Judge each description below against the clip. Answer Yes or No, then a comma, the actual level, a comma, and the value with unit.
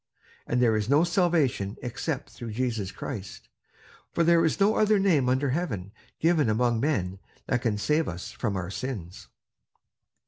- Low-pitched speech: Yes, low, 125 Hz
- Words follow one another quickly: No, average, 160 wpm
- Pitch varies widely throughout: Yes, wide, 7.1 semitones